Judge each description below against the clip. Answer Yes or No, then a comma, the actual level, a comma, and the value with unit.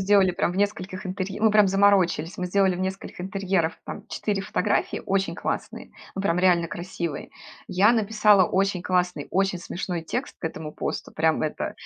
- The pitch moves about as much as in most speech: No, narrow, 1.9 semitones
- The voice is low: No, high, 190 Hz